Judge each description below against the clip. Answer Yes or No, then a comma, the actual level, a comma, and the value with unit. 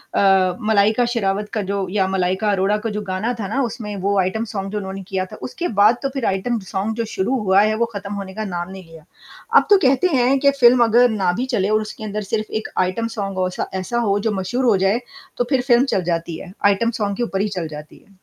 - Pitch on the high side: Yes, high, 205 Hz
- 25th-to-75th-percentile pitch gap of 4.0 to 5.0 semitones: No, average, 3.4 semitones